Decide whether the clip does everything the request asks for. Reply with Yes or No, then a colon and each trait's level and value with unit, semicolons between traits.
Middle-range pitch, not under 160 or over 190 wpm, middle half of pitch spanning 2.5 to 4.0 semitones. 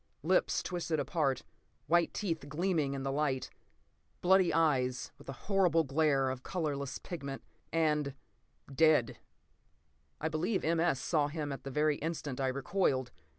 No: medium, 150 Hz; average, 140 wpm; average, 3.3 semitones